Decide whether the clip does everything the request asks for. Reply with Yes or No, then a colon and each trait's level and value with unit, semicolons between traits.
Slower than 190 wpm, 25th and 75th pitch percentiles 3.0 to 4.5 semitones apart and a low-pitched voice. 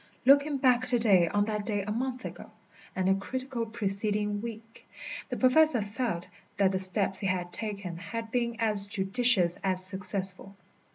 No: average, 165 wpm; average, 3.6 semitones; high, 210 Hz